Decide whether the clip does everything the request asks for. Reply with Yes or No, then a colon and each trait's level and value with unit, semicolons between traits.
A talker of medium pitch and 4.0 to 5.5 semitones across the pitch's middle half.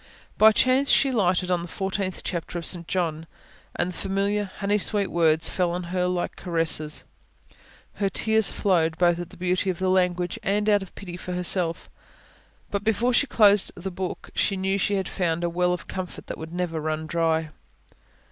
No: medium, 180 Hz; narrow, 2.6 semitones